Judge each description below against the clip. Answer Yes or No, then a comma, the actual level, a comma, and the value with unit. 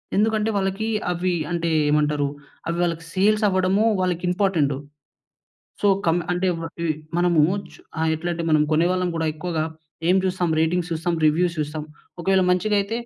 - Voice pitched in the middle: Yes, medium, 175 Hz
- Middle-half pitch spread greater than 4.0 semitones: No, average, 2.7 semitones